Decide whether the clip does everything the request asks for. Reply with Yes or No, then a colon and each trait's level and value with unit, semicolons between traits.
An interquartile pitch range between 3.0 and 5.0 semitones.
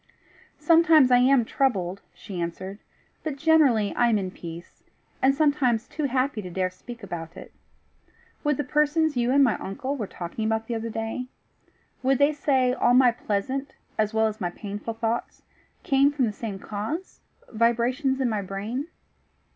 Yes: average, 4.7 semitones